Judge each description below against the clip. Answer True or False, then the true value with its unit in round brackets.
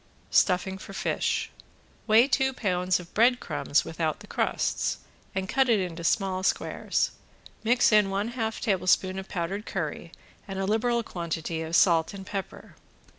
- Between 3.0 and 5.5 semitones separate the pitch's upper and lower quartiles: True (3.5 semitones)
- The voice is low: False (195 Hz)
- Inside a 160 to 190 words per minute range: False (150 wpm)